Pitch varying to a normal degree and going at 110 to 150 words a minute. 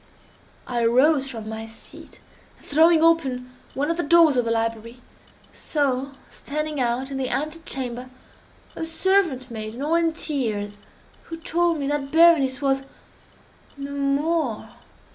Yes: average, 4.4 semitones; average, 140 wpm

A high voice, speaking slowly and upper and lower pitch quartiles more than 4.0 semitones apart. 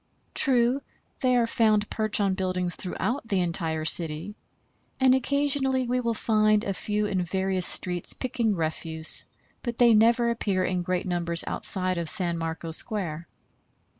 No: high, 200 Hz; average, 150 wpm; average, 5.1 semitones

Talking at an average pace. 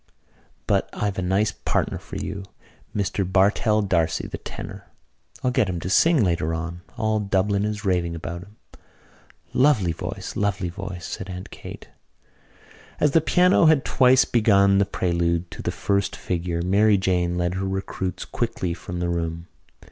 Yes: average, 160 wpm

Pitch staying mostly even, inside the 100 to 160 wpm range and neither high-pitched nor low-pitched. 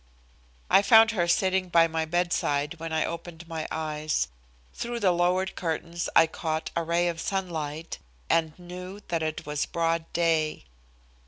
Yes: narrow, 1.9 semitones; average, 155 wpm; medium, 170 Hz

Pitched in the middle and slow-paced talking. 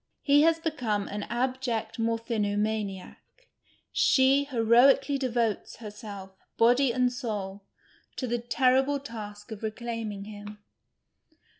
No: high, 230 Hz; slow, 110 wpm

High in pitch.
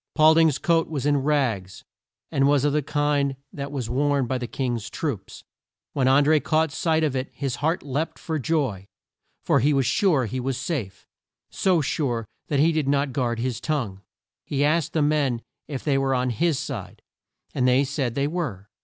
No: medium, 140 Hz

